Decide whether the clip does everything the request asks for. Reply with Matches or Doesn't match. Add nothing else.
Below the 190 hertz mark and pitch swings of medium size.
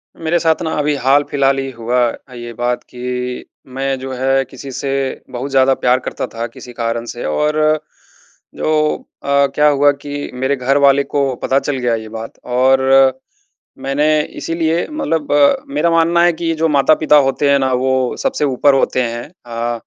Matches